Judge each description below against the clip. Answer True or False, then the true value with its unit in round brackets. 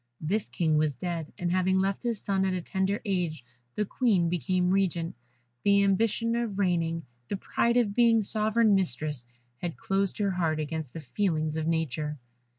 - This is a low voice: False (185 Hz)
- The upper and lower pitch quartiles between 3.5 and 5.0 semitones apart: True (3.9 semitones)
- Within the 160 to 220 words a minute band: True (170 wpm)